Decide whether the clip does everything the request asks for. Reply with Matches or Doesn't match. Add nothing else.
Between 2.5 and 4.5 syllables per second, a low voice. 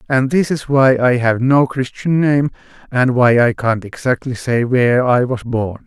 Matches